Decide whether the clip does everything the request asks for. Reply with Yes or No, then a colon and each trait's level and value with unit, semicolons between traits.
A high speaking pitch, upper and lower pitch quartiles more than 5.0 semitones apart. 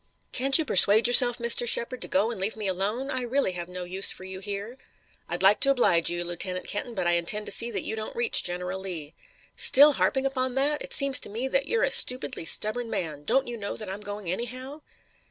Yes: high, 215 Hz; wide, 5.4 semitones